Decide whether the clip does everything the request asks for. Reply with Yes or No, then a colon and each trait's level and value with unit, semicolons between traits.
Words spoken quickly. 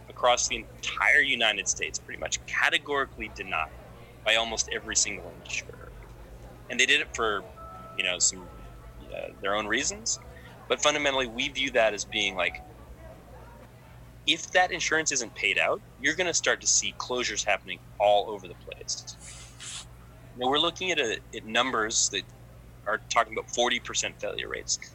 No: average, 160 wpm